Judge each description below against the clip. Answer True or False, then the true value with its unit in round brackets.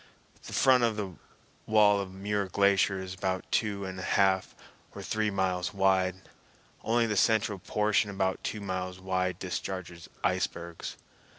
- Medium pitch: False (95 Hz)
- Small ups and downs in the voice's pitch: True (1.8 semitones)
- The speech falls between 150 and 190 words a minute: False (140 wpm)